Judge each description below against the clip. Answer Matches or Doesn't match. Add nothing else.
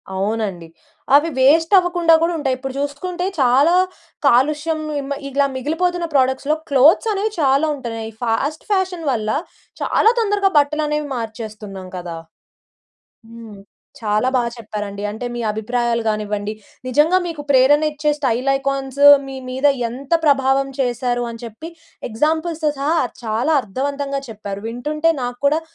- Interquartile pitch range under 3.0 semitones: Doesn't match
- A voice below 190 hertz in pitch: Doesn't match